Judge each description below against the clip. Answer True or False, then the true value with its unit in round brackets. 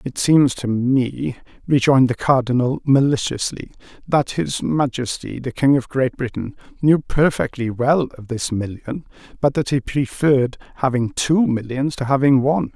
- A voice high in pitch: False (135 Hz)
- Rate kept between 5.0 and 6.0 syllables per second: False (4.6 syllables/s)